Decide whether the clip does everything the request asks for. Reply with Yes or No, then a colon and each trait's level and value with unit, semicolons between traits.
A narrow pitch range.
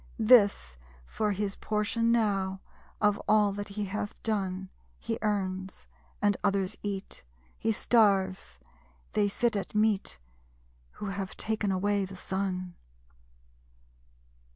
Yes: narrow, 1.8 semitones